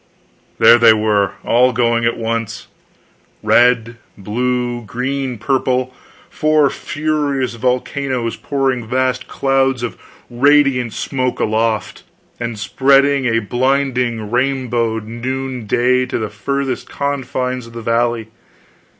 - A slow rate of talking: Yes, slow, 105 wpm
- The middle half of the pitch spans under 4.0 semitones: Yes, narrow, 2.5 semitones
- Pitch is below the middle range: Yes, low, 125 Hz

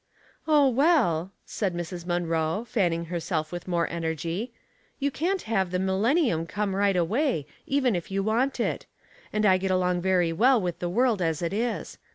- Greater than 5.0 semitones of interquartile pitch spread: Yes, wide, 5.4 semitones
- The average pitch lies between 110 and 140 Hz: No, high, 190 Hz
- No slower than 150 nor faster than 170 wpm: No, average, 185 wpm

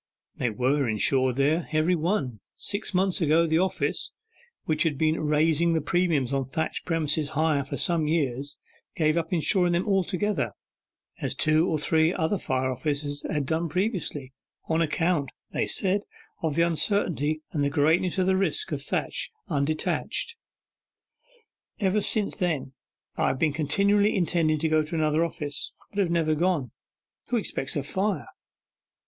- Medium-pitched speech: Yes, medium, 160 Hz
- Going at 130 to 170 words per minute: Yes, average, 155 wpm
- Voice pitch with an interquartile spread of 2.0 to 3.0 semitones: No, average, 3.5 semitones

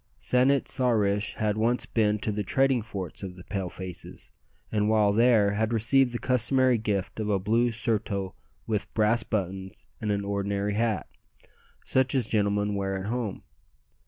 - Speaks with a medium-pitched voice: No, low, 105 Hz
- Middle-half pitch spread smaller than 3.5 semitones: Yes, average, 2.8 semitones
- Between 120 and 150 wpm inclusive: No, average, 170 wpm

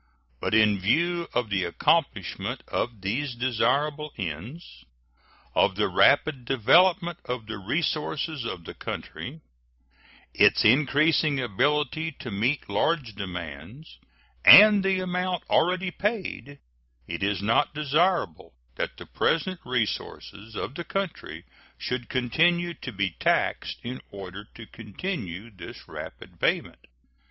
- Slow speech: Yes, slow, 120 wpm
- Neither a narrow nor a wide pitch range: No, wide, 8.0 semitones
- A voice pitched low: Yes, low, 130 Hz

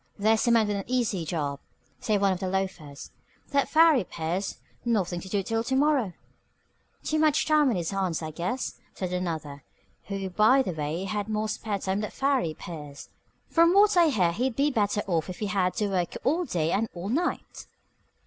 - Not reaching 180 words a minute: No, average, 195 wpm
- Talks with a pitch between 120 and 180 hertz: No, high, 200 Hz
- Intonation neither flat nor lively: No, wide, 6.2 semitones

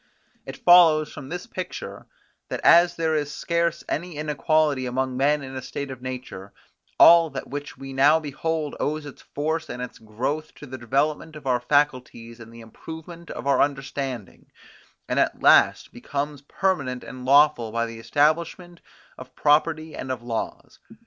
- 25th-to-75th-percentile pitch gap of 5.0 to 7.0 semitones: No, average, 3.6 semitones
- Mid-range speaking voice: Yes, medium, 145 Hz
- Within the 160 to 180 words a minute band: Yes, average, 165 wpm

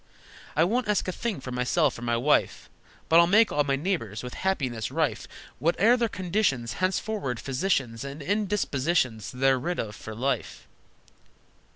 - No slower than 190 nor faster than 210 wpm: No, average, 160 wpm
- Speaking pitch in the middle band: Yes, medium, 145 Hz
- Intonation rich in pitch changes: Yes, wide, 7.3 semitones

